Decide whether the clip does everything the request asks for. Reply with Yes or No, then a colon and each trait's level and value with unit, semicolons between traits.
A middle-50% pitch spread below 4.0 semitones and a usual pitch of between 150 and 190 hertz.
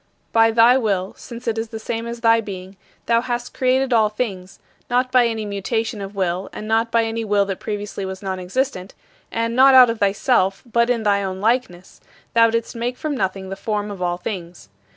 No: average, 3.3 semitones; high, 220 Hz